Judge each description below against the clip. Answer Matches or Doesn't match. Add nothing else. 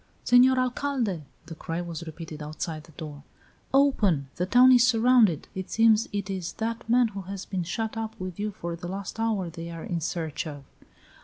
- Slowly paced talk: Doesn't match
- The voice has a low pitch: Doesn't match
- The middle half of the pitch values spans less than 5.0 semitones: Doesn't match